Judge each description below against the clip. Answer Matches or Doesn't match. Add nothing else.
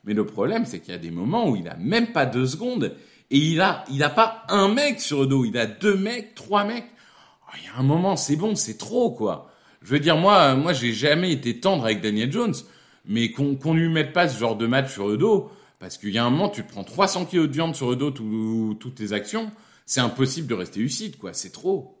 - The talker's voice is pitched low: Doesn't match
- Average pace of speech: Doesn't match